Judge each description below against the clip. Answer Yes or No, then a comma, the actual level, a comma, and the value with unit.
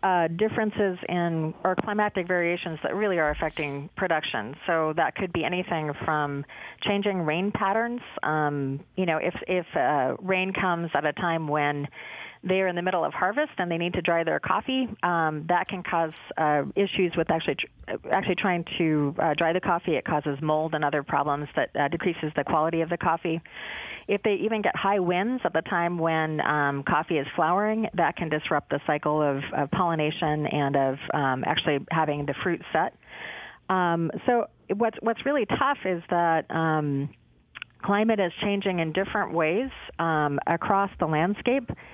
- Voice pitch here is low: No, medium, 170 Hz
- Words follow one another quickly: No, average, 175 wpm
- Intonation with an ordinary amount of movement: Yes, average, 3.8 semitones